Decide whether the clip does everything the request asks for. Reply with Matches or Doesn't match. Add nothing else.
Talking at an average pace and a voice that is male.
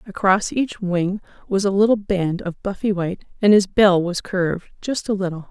Doesn't match